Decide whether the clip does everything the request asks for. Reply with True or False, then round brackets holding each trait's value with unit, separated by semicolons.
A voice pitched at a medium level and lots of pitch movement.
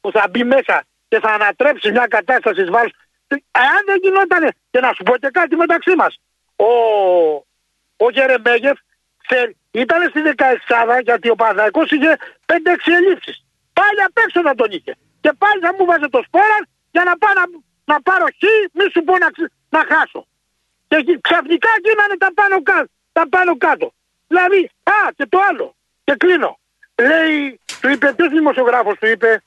False (320 Hz; 6.9 semitones)